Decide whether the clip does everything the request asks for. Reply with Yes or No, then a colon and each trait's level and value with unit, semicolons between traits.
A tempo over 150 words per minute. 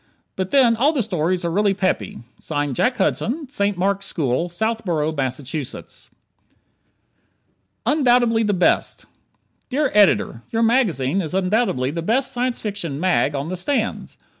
No: slow, 135 wpm